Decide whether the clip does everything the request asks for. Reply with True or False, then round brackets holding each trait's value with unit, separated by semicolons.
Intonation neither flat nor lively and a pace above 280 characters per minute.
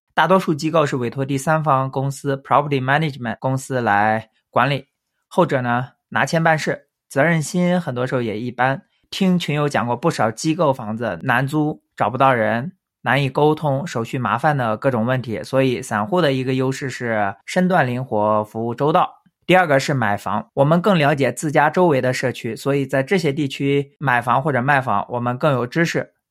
True (4.1 semitones; 315 characters per minute)